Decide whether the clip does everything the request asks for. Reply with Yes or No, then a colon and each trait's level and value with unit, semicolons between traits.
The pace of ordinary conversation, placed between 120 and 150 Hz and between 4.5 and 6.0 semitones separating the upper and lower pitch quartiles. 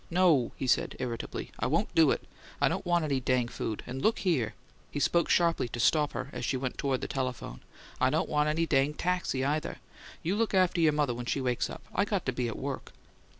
No: fast, 230 wpm; medium, 140 Hz; average, 4.8 semitones